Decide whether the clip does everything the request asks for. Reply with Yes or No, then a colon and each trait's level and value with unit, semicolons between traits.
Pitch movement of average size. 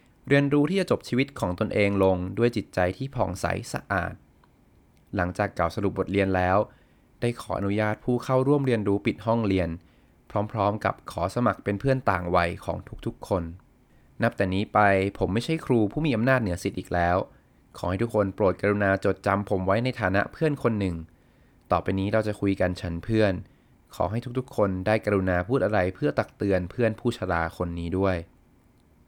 Yes: average, 3.9 semitones